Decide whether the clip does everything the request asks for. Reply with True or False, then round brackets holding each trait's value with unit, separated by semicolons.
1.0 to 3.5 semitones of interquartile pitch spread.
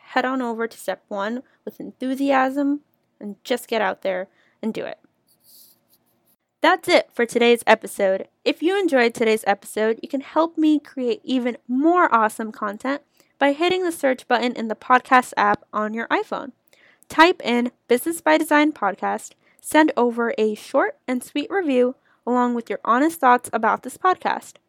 False (4.7 semitones)